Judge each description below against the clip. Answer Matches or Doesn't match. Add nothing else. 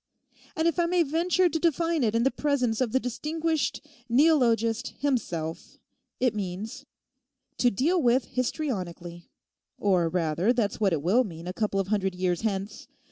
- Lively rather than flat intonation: Matches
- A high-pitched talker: Matches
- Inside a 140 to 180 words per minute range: Matches